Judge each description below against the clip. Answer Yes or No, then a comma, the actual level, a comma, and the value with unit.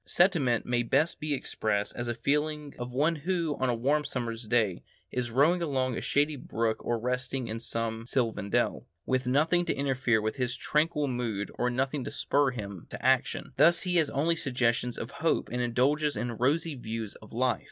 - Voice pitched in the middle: No, low, 130 Hz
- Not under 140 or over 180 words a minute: No, average, 195 wpm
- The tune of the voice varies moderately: Yes, average, 4.1 semitones